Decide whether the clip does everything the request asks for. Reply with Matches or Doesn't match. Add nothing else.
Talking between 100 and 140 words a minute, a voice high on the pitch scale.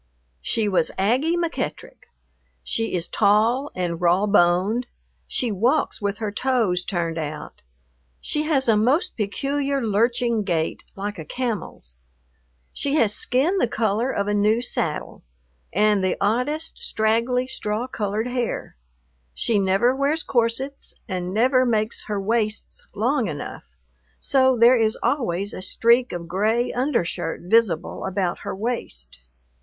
Matches